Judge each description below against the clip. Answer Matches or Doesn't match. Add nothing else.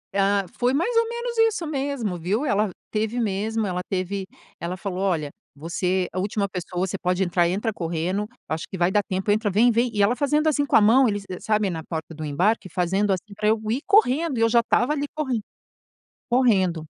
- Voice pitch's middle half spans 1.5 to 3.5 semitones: Doesn't match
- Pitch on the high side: Matches